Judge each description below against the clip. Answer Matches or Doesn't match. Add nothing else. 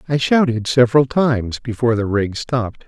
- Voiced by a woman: Doesn't match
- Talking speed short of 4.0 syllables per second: Doesn't match